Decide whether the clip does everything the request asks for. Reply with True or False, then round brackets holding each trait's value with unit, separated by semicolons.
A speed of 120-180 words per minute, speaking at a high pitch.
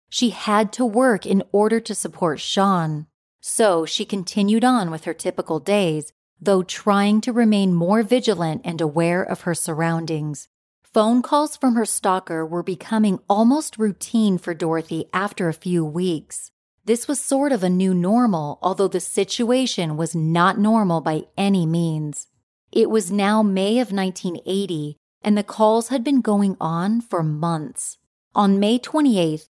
True (155 wpm; 195 Hz)